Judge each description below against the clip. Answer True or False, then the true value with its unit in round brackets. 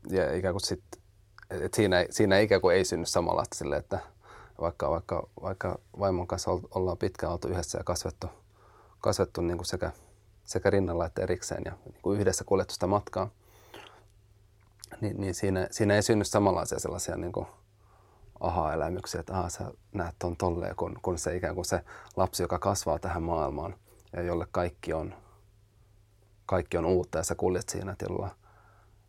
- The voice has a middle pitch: False (95 Hz)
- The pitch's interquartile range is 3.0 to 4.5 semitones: False (2.4 semitones)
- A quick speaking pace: True (160 wpm)